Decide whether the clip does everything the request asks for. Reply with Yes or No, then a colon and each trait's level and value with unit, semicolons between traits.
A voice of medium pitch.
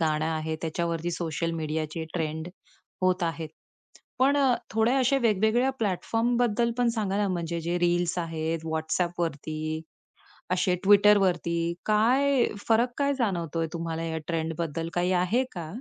Yes: medium, 175 Hz